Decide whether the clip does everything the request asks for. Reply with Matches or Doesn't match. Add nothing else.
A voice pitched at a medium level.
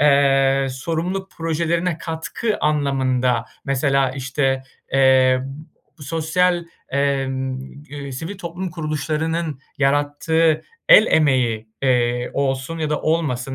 Matches